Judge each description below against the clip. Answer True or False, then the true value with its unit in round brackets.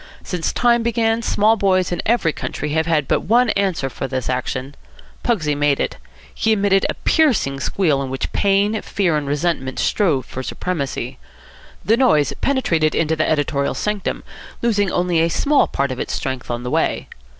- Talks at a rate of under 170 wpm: False (175 wpm)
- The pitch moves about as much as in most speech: False (6.9 semitones)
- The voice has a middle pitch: True (170 Hz)